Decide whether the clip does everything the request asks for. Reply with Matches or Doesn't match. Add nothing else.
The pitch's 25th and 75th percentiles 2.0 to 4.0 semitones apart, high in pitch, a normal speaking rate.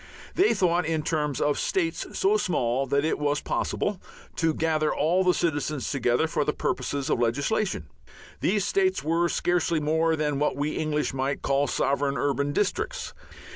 Doesn't match